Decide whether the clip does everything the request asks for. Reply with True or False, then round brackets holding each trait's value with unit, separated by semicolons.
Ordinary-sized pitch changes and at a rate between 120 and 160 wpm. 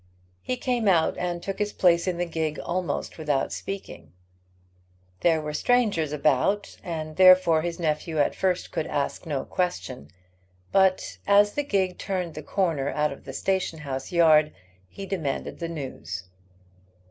True (3.9 semitones; 155 wpm)